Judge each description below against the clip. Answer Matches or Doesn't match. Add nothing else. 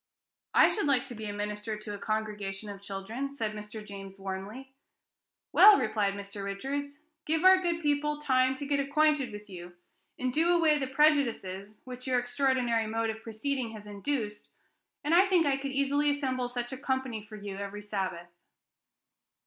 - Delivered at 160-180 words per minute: Matches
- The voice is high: Matches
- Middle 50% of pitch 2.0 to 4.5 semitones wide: Doesn't match